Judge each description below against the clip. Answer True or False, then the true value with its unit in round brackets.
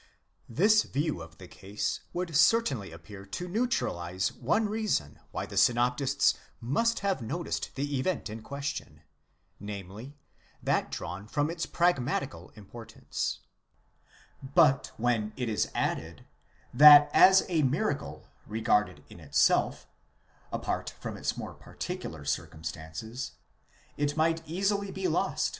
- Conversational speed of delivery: False (125 wpm)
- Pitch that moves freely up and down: True (8.1 semitones)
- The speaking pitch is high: False (135 Hz)